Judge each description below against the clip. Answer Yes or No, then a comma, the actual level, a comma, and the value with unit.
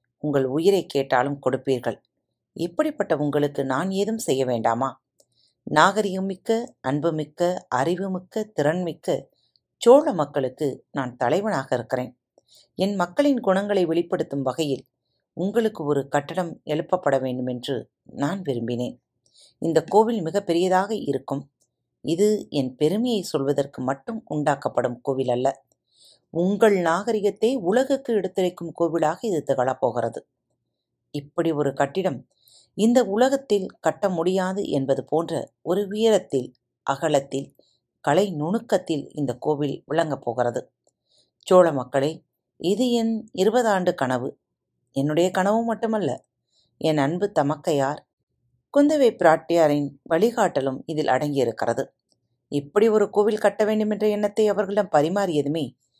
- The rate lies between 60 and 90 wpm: No, average, 105 wpm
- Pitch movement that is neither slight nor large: No, wide, 6.6 semitones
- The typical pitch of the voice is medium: Yes, medium, 160 Hz